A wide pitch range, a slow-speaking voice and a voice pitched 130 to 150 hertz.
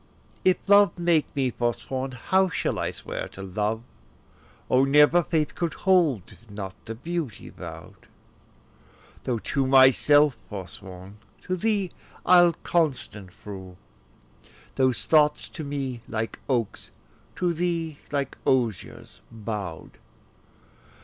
Yes: wide, 7.3 semitones; slow, 115 wpm; low, 135 Hz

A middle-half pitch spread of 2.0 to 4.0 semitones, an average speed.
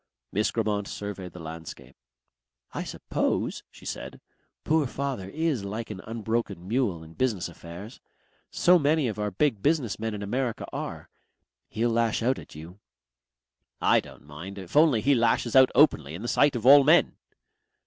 No: wide, 5.4 semitones; average, 170 wpm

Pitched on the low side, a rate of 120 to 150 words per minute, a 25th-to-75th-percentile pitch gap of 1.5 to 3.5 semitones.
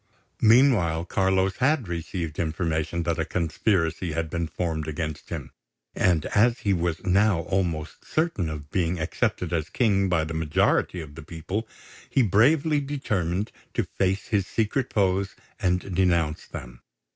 No: very low, 90 Hz; average, 145 wpm; average, 3.9 semitones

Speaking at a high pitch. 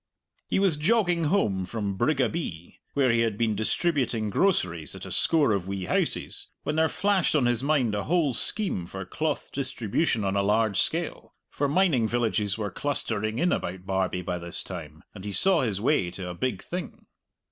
No: low, 115 Hz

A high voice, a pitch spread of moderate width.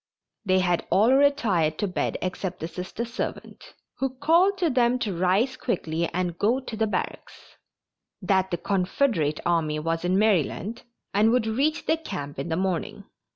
No: high, 195 Hz; wide, 6.0 semitones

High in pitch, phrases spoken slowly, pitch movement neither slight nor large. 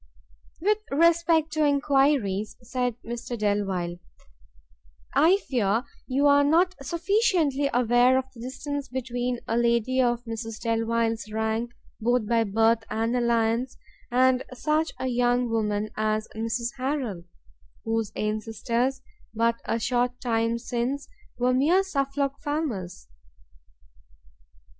Yes: high, 245 Hz; slow, 115 wpm; average, 3.5 semitones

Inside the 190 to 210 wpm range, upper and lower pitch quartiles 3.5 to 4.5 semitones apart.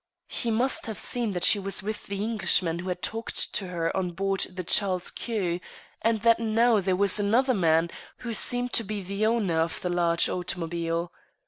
Yes: average, 195 wpm; average, 4.0 semitones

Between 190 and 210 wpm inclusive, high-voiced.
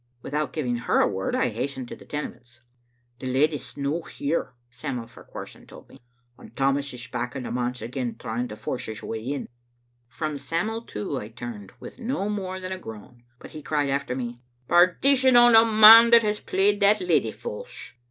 No: average, 200 wpm; medium, 140 Hz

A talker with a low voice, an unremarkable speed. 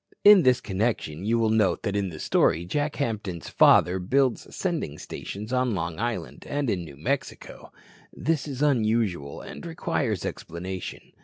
Yes: low, 110 Hz; average, 155 wpm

